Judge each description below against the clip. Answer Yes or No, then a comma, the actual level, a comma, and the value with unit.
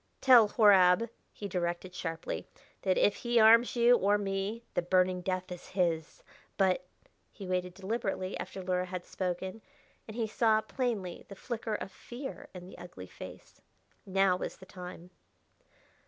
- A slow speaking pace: No, average, 155 wpm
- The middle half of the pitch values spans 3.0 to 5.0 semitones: Yes, average, 3.3 semitones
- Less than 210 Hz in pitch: Yes, high, 190 Hz